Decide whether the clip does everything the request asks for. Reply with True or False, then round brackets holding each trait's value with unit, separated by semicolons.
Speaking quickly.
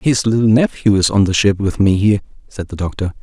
True (240 wpm)